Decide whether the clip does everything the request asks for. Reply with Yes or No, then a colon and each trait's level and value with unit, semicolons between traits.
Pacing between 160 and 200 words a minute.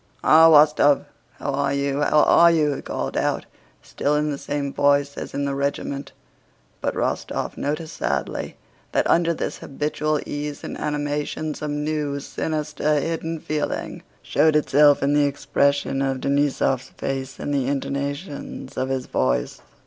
No: average, 150 wpm